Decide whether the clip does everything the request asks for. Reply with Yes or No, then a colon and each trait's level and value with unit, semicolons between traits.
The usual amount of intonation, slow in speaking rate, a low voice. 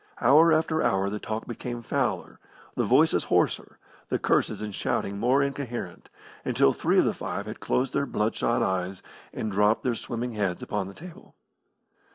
No: average, 4.4 semitones; average, 175 wpm; low, 110 Hz